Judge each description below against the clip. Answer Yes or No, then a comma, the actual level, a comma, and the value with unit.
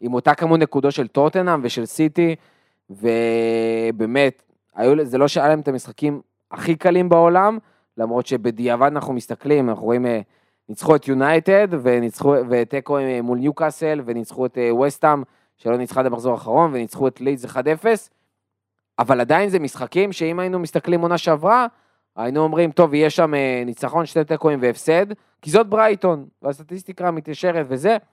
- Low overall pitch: No, medium, 145 Hz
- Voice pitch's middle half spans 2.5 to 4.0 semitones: No, wide, 5.4 semitones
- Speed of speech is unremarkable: Yes, average, 140 wpm